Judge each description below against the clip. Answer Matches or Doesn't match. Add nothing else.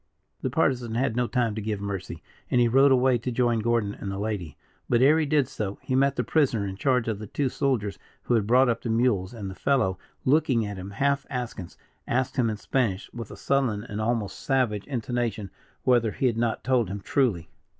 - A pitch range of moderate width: Matches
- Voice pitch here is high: Doesn't match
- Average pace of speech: Doesn't match